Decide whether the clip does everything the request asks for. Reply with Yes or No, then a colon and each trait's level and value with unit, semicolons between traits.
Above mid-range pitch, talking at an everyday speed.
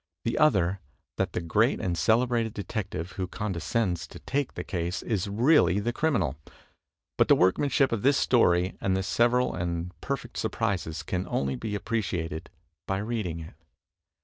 No: very low, 95 Hz; average, 165 wpm